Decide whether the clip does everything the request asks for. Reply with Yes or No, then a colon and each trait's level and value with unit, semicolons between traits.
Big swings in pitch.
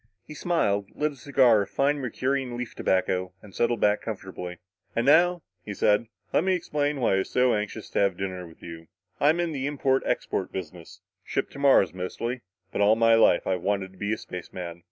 Yes: wide, 6.6 semitones